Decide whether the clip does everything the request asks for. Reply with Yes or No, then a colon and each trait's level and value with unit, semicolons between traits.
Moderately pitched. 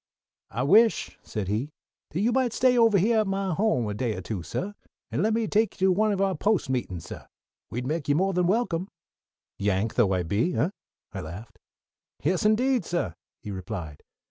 Yes: medium, 175 Hz